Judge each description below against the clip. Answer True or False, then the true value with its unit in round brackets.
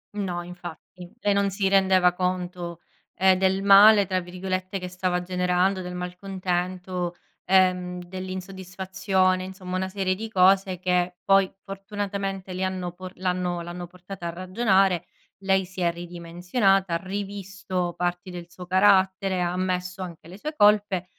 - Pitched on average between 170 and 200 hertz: True (185 Hz)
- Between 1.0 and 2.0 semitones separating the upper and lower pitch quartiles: True (1.3 semitones)